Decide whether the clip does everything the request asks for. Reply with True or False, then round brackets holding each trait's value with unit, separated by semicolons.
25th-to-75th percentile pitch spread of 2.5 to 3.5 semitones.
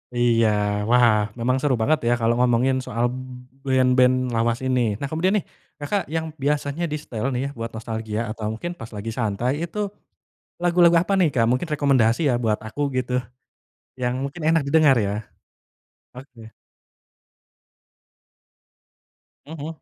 False (4.5 semitones)